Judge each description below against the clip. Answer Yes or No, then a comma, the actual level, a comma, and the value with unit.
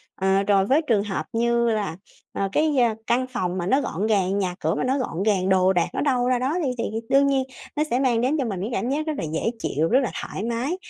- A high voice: Yes, high, 230 Hz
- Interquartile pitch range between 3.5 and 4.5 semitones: No, average, 5.2 semitones